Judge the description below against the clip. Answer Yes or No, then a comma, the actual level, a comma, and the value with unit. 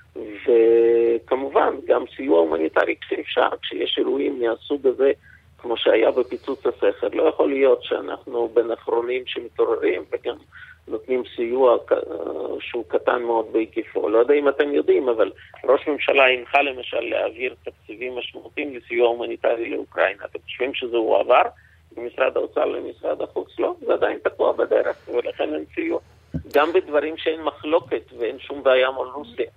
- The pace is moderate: Yes, average, 140 wpm